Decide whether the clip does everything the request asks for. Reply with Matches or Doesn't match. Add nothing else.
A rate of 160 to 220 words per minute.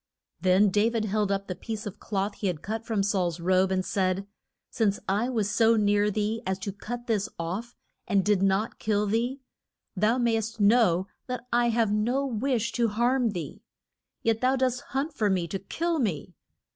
Matches